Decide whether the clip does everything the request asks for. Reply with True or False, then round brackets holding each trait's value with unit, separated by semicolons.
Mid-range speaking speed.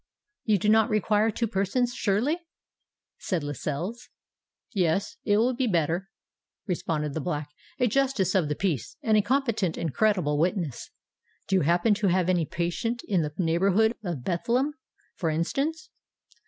True (150 wpm)